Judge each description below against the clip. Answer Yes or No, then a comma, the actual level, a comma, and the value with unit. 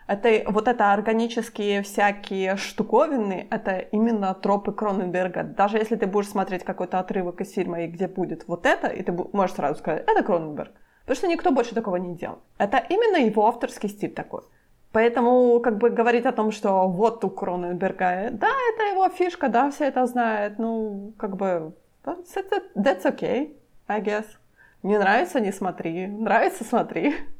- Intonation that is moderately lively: Yes, average, 4.3 semitones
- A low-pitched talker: No, high, 215 Hz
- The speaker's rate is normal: No, fast, 165 wpm